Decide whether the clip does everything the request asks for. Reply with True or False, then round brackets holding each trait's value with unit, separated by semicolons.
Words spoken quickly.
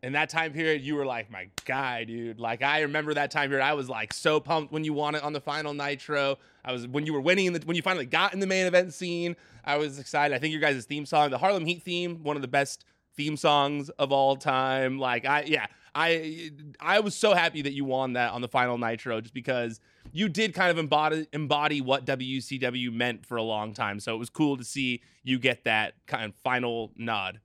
True (245 wpm)